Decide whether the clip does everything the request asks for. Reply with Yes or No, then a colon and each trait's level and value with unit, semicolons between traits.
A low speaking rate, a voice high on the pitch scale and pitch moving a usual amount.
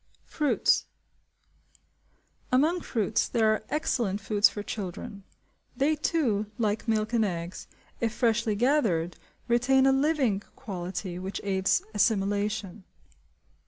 Yes: slow, 110 wpm; high, 215 Hz; average, 4.2 semitones